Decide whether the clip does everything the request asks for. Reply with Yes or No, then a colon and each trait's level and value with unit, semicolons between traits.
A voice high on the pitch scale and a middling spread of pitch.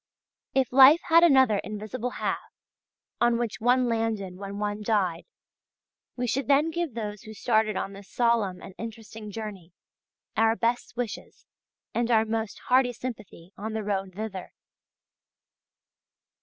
Yes: high, 220 Hz; average, 3.0 semitones